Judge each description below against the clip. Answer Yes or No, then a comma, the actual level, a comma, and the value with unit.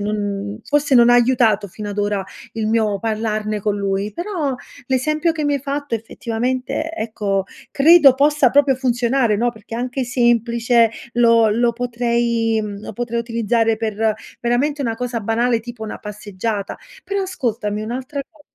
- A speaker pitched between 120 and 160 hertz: No, high, 235 Hz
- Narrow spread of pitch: No, average, 3.1 semitones